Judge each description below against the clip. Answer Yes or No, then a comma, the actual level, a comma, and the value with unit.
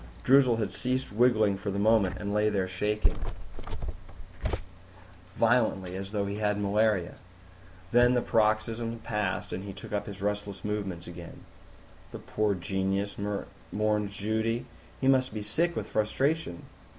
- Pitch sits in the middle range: No, low, 105 Hz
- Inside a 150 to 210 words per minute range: No, average, 140 wpm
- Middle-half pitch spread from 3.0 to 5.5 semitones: No, narrow, 2.4 semitones